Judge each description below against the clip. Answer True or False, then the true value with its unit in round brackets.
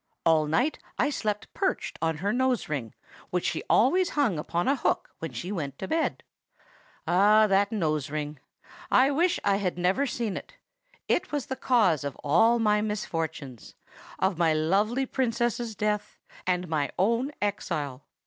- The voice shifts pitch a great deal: True (6.8 semitones)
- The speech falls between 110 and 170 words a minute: True (160 wpm)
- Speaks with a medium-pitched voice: False (200 Hz)